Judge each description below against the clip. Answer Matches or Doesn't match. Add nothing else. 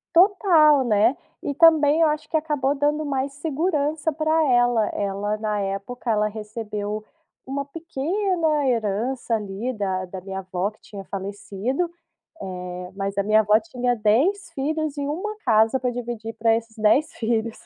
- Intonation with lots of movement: Matches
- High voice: Matches